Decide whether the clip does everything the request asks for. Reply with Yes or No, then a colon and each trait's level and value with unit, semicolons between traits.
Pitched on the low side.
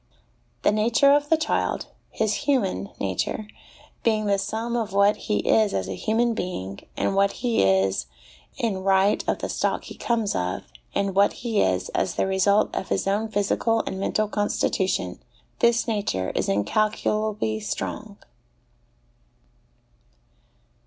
No: high, 205 Hz